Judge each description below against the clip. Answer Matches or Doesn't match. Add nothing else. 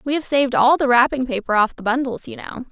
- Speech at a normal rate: Doesn't match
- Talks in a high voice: Matches